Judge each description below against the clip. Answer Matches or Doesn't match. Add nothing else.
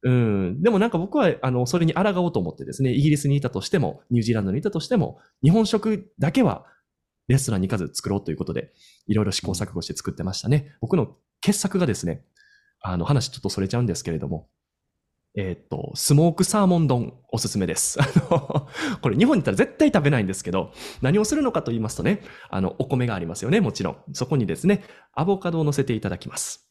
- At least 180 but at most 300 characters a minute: Doesn't match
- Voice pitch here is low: Matches